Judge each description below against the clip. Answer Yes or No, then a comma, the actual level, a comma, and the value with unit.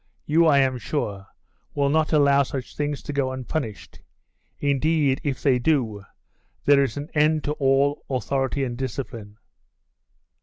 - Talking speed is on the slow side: No, average, 145 wpm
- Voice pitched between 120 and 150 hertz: Yes, medium, 140 Hz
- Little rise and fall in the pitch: Yes, narrow, 2.1 semitones